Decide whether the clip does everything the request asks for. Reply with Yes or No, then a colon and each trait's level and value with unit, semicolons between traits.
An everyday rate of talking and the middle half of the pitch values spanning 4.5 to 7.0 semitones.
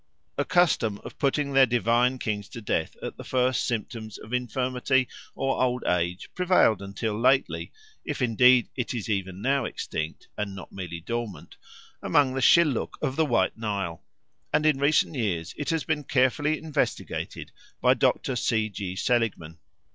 Yes: average, 160 wpm; average, 4.8 semitones